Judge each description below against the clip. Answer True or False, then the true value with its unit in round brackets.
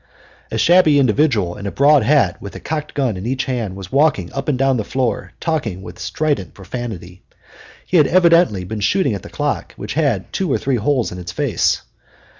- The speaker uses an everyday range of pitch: False (7.0 semitones)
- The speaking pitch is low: True (130 Hz)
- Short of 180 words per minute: False (205 wpm)